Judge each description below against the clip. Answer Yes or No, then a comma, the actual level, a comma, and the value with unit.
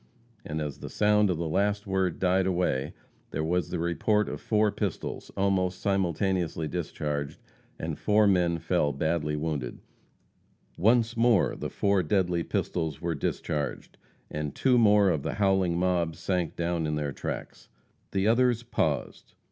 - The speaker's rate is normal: Yes, average, 150 wpm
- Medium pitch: No, very low, 90 Hz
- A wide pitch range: No, average, 4.1 semitones